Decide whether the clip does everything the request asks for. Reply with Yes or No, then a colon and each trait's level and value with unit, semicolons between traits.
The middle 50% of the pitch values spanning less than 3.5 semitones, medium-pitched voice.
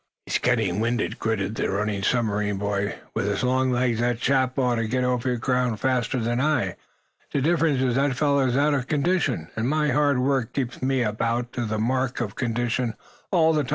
No: average, 3.0 semitones; low, 125 Hz